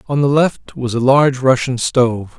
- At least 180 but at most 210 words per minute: Yes, average, 200 wpm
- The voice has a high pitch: No, low, 130 Hz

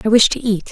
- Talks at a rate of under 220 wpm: No, fast, 340 wpm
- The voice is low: No, high, 225 Hz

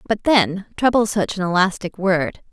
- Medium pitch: No, high, 195 Hz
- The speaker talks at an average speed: Yes, average, 190 wpm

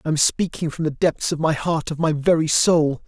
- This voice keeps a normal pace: No, fast, 235 wpm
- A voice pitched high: No, medium, 155 Hz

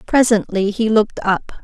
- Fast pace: No, average, 145 wpm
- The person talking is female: Yes, female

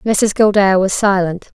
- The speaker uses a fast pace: No, average, 150 wpm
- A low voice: No, high, 195 Hz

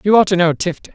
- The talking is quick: Yes, fast, 315 wpm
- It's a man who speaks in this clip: No, female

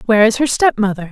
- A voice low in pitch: No, high, 225 Hz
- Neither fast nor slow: No, fast, 215 wpm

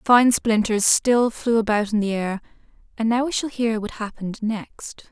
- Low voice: No, high, 220 Hz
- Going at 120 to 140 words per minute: No, average, 200 wpm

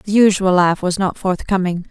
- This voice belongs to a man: No, female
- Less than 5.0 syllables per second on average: Yes, 4.8 syllables/s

